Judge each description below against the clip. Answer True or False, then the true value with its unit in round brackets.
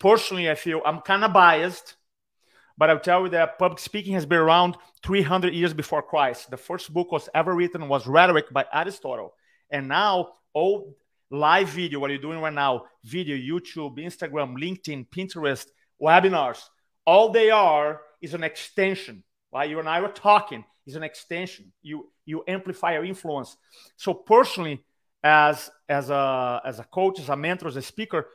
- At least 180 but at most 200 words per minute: False (165 wpm)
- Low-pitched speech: False (165 Hz)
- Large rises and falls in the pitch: False (3.7 semitones)